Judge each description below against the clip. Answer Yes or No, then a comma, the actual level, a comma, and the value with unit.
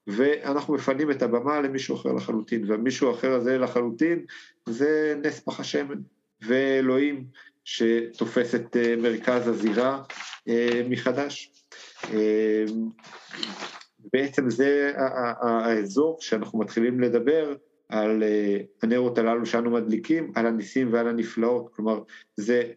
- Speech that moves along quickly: No, slow, 100 wpm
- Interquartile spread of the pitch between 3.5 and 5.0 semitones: No, average, 3.1 semitones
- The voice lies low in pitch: Yes, low, 120 Hz